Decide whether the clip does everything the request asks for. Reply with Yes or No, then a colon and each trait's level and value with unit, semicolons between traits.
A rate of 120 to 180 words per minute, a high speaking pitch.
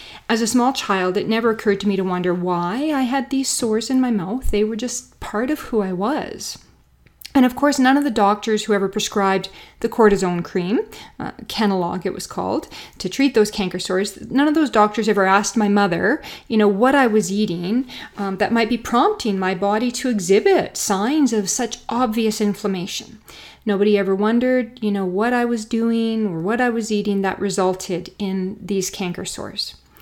No: average, 195 wpm; high, 215 Hz